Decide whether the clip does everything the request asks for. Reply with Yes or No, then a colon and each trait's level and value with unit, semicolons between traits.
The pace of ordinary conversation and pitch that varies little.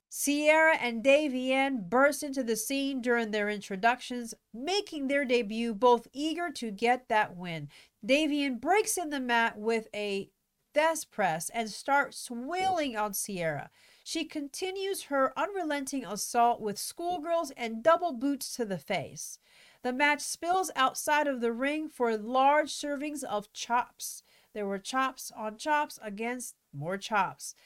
No: average, 145 wpm; average, 4.7 semitones